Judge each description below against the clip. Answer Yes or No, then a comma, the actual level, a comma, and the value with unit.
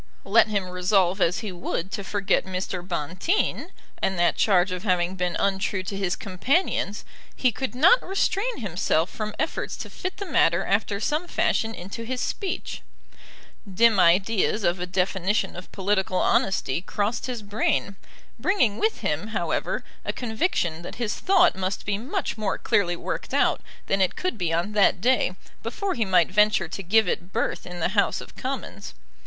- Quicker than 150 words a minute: Yes, average, 170 wpm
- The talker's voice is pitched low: No, high, 200 Hz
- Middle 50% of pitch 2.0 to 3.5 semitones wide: No, average, 4.0 semitones